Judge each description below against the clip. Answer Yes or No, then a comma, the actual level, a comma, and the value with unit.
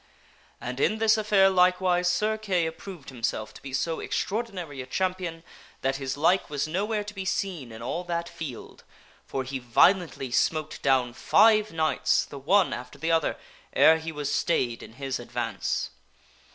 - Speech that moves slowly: No, average, 170 wpm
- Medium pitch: Yes, medium, 160 Hz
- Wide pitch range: Yes, wide, 5.9 semitones